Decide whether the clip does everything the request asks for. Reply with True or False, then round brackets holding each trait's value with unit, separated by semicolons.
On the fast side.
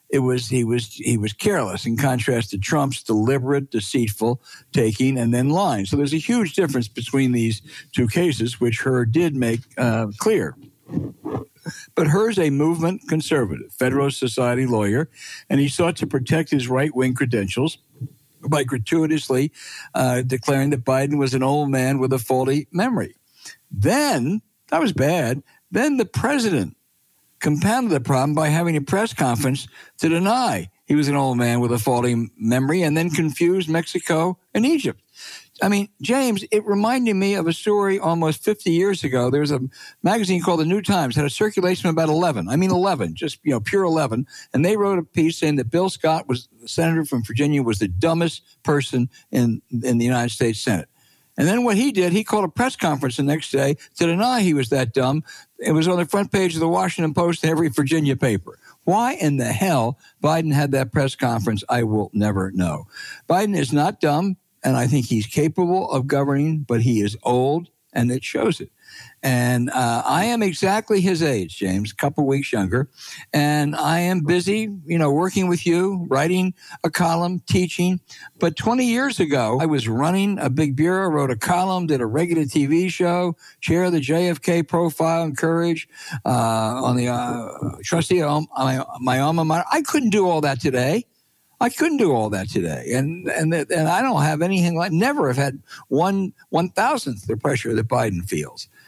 False (190 wpm)